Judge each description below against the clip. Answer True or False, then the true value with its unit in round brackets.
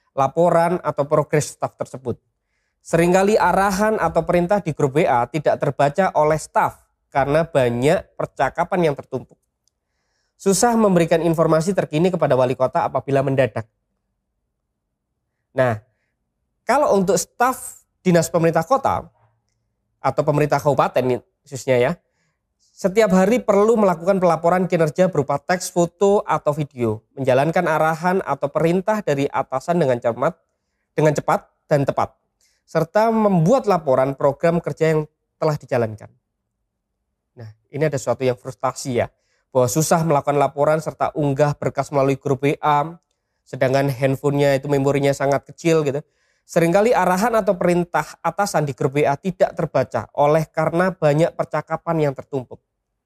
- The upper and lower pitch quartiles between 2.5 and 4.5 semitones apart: True (4.1 semitones)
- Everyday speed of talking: True (130 wpm)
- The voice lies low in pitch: False (150 Hz)